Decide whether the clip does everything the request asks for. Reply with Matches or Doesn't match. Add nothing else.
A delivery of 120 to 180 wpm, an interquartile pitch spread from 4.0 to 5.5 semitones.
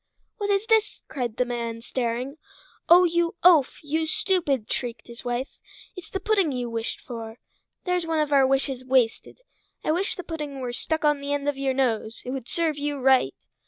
Doesn't match